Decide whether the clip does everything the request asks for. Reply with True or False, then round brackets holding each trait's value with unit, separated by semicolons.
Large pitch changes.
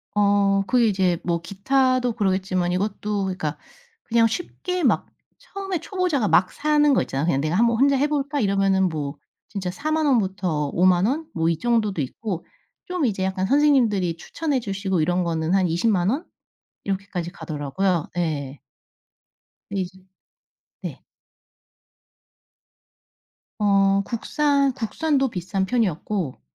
True (6.2 semitones)